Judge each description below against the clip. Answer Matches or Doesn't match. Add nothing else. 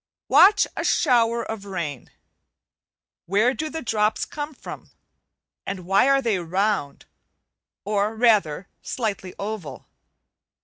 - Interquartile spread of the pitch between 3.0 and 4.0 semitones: Matches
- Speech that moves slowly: Matches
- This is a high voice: Matches